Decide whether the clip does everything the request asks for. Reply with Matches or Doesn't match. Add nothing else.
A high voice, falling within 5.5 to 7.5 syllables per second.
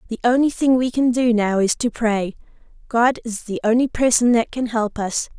Doesn't match